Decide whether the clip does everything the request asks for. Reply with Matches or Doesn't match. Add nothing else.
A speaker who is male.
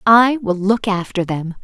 Doesn't match